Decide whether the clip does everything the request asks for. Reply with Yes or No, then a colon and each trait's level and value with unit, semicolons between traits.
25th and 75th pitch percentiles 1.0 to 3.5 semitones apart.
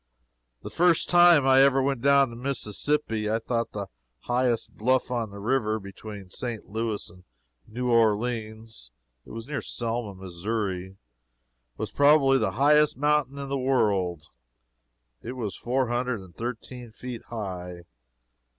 No: average, 4.2 semitones